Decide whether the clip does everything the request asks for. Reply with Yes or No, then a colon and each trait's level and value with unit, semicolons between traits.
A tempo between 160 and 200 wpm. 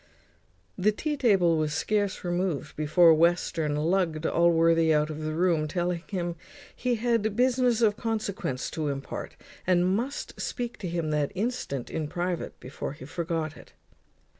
No: average, 150 wpm